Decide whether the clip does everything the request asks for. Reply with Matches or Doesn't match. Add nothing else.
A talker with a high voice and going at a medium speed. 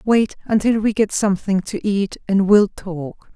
Matches